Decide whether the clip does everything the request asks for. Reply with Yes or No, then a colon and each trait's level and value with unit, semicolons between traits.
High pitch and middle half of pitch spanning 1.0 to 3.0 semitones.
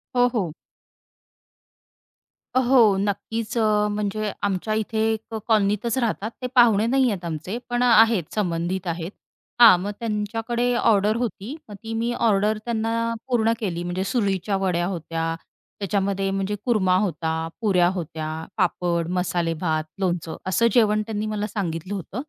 No: high, 205 Hz; average, 3.7 semitones